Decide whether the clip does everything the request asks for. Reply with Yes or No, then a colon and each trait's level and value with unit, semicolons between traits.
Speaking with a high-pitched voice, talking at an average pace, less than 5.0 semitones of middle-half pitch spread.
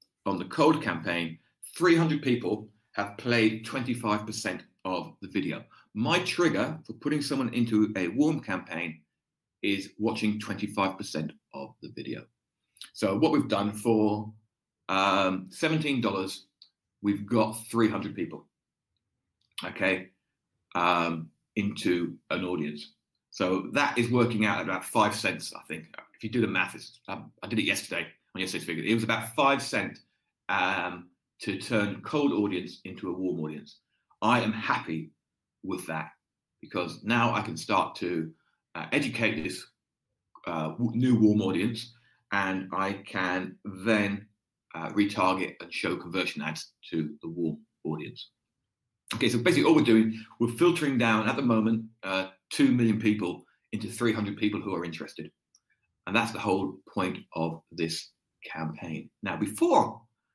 No: low, 105 Hz; average, 145 wpm; average, 3.6 semitones